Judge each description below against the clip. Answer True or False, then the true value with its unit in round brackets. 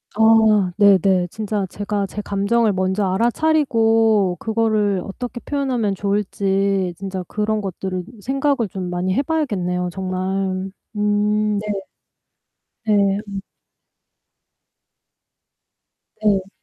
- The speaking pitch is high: True (205 Hz)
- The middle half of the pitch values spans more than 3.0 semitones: False (2.5 semitones)